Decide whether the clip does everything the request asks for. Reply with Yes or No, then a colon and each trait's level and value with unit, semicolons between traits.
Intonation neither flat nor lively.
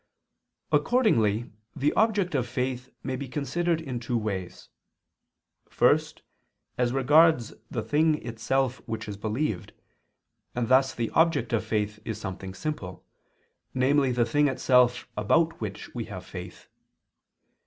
Yes: average, 4.8 semitones